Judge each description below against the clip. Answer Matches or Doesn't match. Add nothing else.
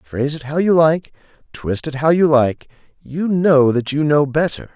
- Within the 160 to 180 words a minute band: Doesn't match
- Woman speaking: Doesn't match